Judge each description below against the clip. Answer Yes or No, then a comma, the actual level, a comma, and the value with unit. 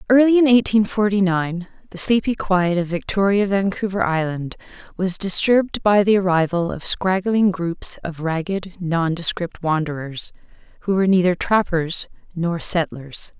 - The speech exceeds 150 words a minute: No, slow, 135 wpm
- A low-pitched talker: No, medium, 185 Hz